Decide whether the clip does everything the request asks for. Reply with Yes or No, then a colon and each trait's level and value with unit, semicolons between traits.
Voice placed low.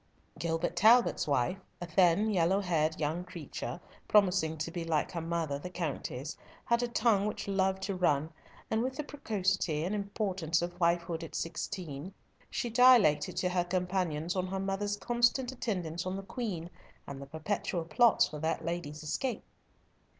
No: medium, 180 Hz